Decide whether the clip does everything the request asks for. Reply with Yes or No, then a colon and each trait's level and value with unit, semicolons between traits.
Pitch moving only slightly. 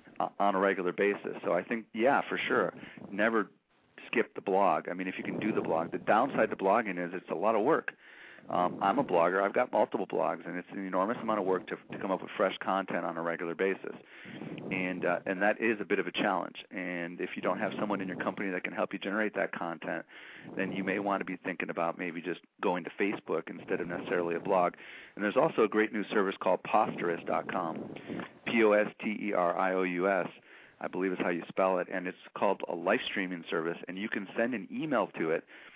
Yes: narrow, 2.1 semitones